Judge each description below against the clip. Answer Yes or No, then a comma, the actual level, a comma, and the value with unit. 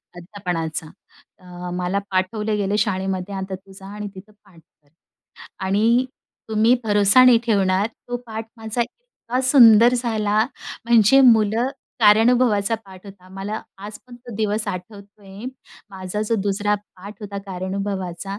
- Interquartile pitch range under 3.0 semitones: Yes, narrow, 2.6 semitones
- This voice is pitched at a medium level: No, high, 205 Hz